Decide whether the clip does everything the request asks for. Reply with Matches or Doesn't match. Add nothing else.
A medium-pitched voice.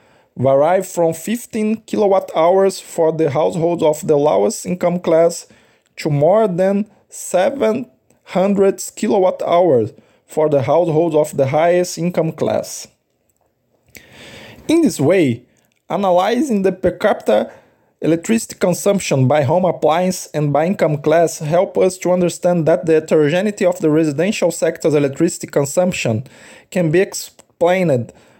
Matches